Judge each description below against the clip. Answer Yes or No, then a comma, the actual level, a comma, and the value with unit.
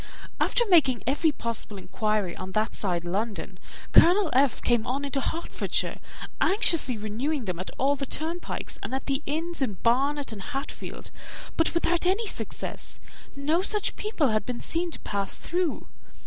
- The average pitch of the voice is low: No, very high, 275 Hz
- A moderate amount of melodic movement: No, wide, 7.3 semitones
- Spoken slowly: No, average, 160 wpm